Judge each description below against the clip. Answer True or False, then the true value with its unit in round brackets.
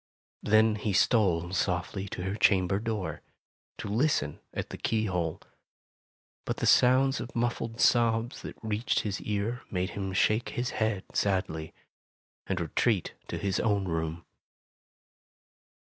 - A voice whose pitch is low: True (105 Hz)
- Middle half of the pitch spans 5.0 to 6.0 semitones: False (3.4 semitones)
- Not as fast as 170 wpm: True (135 wpm)